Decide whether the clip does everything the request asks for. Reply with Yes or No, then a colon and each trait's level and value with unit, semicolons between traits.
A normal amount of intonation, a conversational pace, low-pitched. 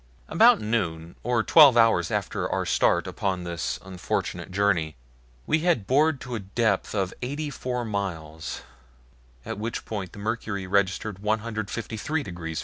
Yes: average, 4.2 semitones; average, 145 wpm; low, 105 Hz